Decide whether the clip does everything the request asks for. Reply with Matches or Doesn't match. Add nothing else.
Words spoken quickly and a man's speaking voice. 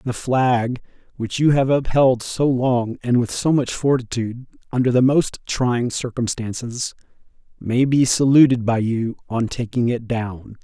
Doesn't match